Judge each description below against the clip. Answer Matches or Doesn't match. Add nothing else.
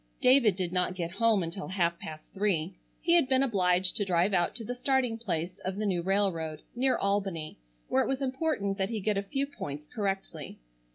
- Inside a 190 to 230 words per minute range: Matches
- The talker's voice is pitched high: Matches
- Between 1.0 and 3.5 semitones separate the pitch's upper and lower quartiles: Doesn't match